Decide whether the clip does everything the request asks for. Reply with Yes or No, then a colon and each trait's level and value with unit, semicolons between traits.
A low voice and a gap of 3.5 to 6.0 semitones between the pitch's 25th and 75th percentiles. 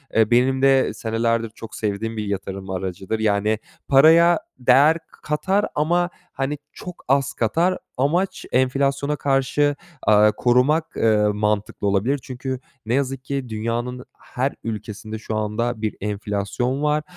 Yes: low, 125 Hz; average, 4.5 semitones